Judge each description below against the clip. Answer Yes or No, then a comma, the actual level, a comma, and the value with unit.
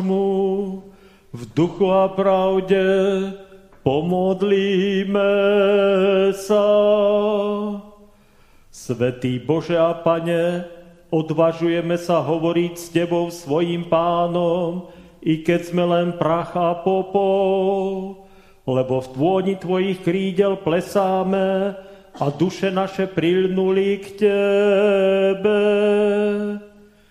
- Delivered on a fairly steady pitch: Yes, narrow, 2.3 semitones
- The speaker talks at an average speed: No, slow, 80 wpm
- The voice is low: No, high, 190 Hz